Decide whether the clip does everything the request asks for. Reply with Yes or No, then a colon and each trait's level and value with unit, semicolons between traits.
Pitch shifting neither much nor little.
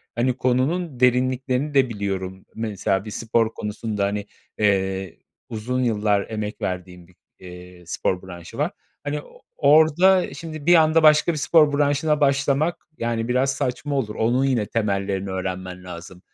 No: wide, 6.6 semitones